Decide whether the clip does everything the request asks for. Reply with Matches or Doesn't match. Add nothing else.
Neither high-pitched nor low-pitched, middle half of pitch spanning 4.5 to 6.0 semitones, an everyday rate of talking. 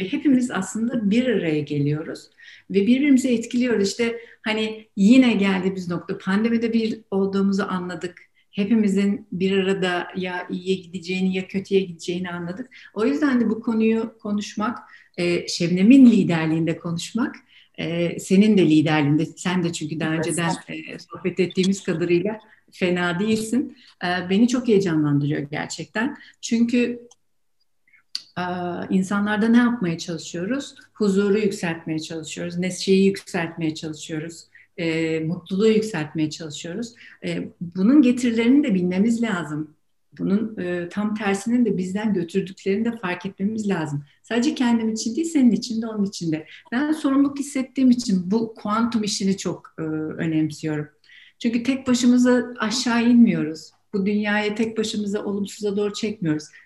Doesn't match